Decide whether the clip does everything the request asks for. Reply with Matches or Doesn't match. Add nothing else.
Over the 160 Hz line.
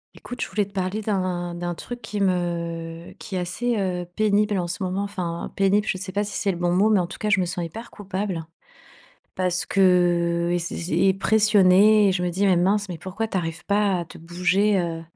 Matches